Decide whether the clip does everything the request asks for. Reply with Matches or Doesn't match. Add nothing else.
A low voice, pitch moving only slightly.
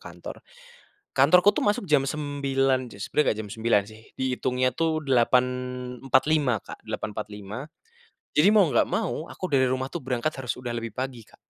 Doesn't match